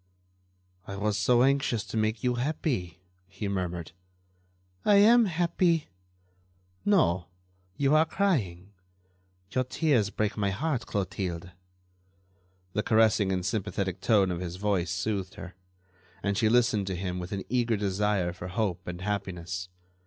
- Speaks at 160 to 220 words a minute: No, average, 140 wpm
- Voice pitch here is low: Yes, low, 100 Hz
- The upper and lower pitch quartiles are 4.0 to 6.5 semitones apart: Yes, average, 4.9 semitones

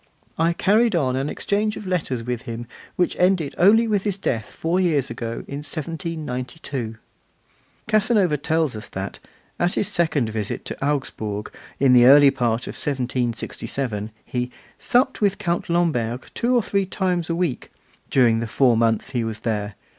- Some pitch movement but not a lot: No, wide, 7.1 semitones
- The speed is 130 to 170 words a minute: Yes, average, 160 wpm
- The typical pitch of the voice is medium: Yes, medium, 145 Hz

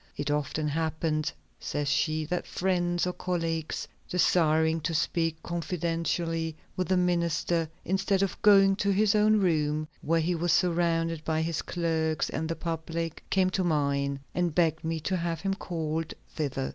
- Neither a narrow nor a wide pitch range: No, narrow, 2.1 semitones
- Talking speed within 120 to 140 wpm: No, average, 160 wpm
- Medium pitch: Yes, medium, 165 Hz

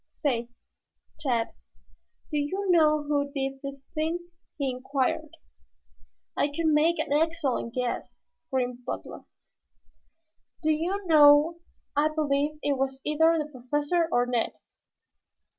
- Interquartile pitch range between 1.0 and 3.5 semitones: Yes, average, 2.8 semitones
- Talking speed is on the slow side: Yes, slow, 120 wpm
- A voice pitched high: Yes, very high, 290 Hz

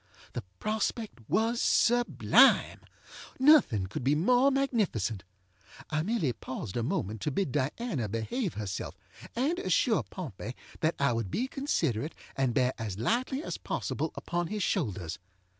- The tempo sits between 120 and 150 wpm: Yes, average, 140 wpm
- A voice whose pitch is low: No, medium, 155 Hz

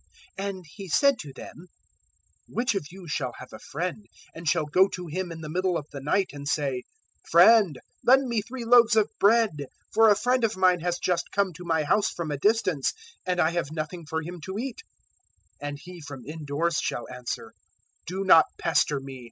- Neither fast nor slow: No, fast, 210 wpm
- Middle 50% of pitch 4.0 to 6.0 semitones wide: Yes, average, 4.9 semitones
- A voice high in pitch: No, medium, 175 Hz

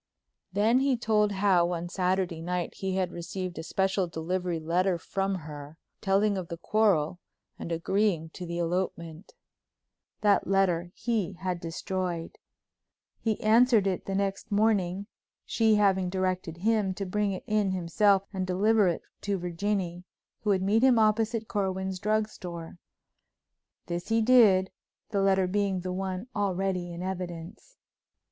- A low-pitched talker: No, high, 190 Hz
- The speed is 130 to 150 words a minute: Yes, average, 145 wpm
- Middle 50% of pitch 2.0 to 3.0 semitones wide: Yes, average, 2.7 semitones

